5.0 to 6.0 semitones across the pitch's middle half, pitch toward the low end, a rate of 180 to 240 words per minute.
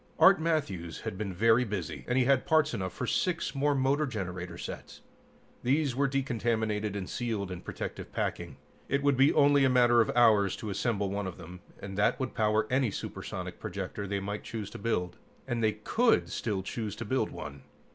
Yes: average, 5.3 semitones; low, 110 Hz; average, 195 wpm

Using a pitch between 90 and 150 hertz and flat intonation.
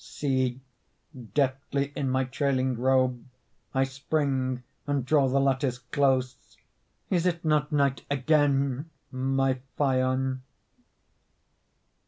Yes: low, 135 Hz; narrow, 1.6 semitones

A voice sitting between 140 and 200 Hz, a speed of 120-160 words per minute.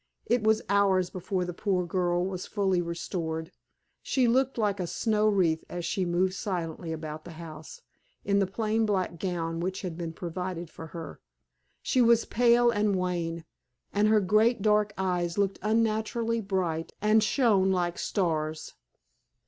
Yes: high, 190 Hz; average, 155 wpm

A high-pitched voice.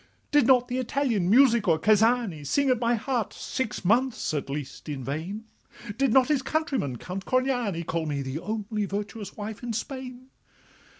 Yes: high, 225 Hz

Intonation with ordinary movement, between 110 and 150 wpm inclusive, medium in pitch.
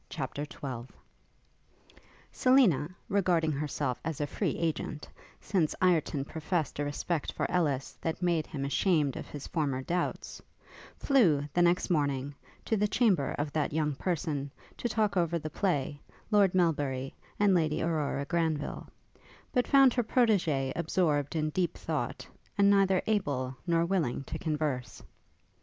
Yes: average, 4.2 semitones; average, 145 wpm; medium, 160 Hz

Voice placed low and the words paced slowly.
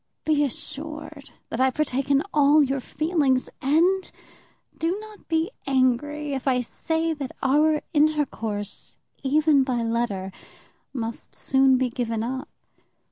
No: very high, 275 Hz; slow, 130 wpm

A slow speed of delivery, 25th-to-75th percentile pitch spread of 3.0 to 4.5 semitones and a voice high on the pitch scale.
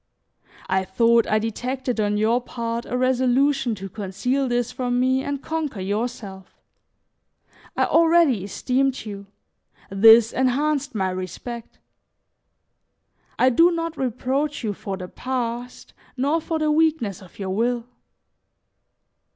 Yes: slow, 125 wpm; average, 4.2 semitones; high, 245 Hz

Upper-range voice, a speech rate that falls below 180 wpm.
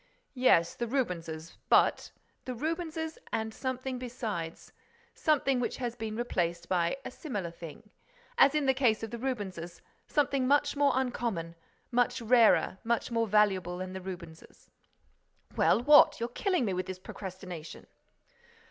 Yes: high, 230 Hz; average, 140 wpm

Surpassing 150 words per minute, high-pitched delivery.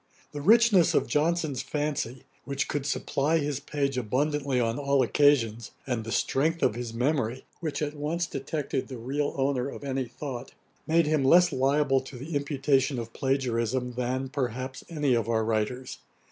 No: average, 165 wpm; low, 135 Hz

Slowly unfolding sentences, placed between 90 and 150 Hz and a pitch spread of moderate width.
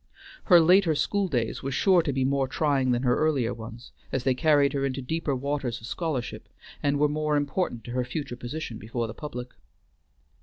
No: average, 195 wpm; low, 135 Hz; average, 3.6 semitones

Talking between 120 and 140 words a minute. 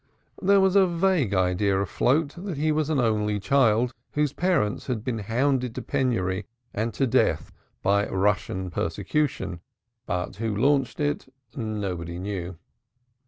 Yes: slow, 135 wpm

